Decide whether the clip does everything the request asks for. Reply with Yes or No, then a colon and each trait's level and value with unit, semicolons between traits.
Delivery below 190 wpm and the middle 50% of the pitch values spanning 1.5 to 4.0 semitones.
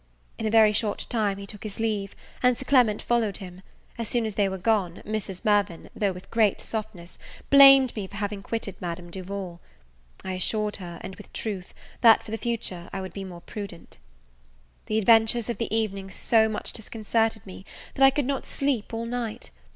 No: average, 195 wpm; average, 2.8 semitones